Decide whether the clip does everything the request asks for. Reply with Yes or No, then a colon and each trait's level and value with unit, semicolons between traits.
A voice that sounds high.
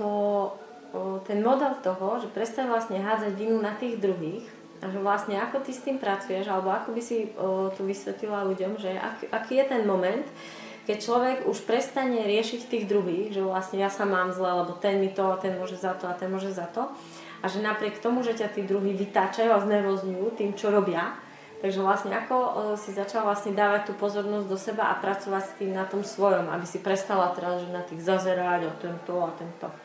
Yes: high, 200 Hz